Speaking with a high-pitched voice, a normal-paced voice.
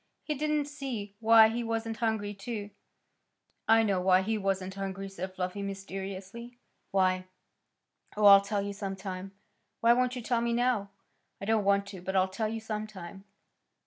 Yes: high, 205 Hz; average, 175 wpm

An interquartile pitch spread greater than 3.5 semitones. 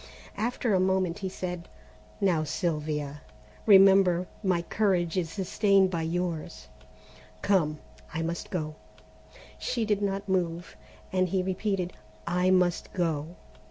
No: narrow, 2.6 semitones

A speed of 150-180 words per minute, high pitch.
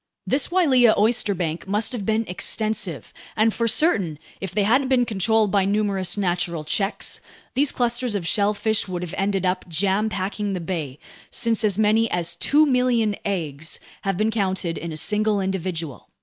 Yes: average, 165 wpm; high, 205 Hz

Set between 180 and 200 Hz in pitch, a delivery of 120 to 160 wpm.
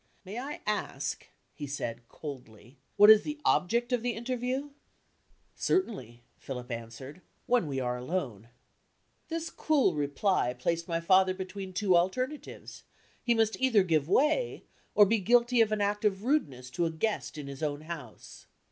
Yes: medium, 185 Hz; average, 155 wpm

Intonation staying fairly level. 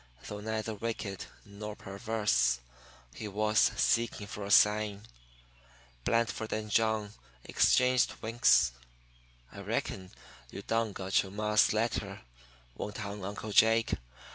Yes: narrow, 1.8 semitones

